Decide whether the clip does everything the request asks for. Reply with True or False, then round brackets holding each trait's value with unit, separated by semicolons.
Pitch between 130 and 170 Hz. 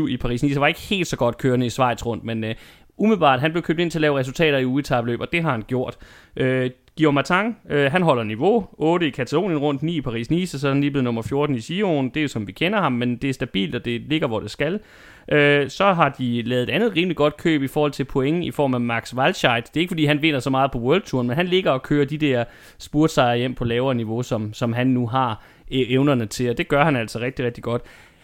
True (135 Hz)